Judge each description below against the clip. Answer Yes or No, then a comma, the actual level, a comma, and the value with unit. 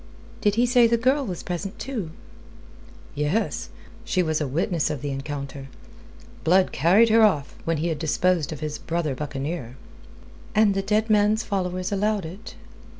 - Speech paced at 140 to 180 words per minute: Yes, average, 160 wpm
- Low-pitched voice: No, medium, 180 Hz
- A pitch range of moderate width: No, wide, 5.8 semitones